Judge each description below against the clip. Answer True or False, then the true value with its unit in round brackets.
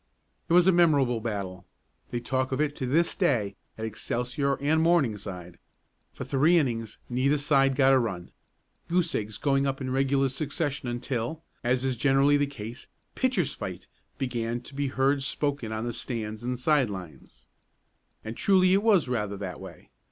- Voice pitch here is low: True (130 Hz)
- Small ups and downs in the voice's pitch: False (4.1 semitones)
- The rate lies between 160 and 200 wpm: True (170 wpm)